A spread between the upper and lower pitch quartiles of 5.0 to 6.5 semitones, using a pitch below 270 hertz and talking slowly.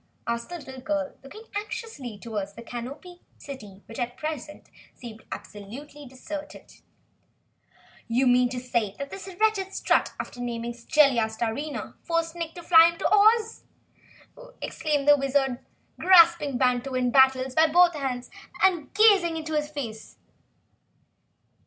No: wide, 5.4 semitones; very high, 280 Hz; slow, 130 wpm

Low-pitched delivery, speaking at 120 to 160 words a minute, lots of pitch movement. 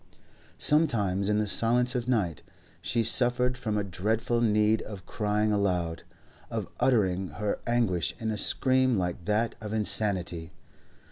No: low, 105 Hz; average, 140 wpm; average, 3.5 semitones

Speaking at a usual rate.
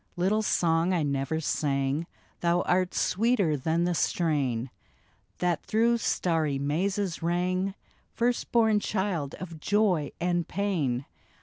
No: slow, 120 wpm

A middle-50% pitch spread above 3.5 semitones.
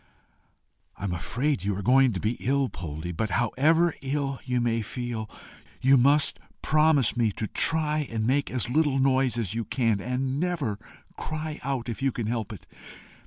Yes: average, 4.0 semitones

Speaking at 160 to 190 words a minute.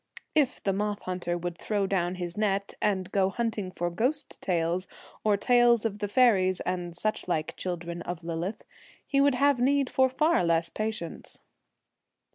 Yes: average, 165 wpm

